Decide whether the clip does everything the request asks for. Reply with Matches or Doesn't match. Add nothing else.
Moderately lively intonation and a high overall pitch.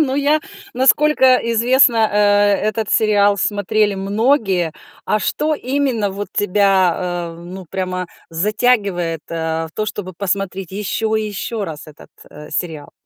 Matches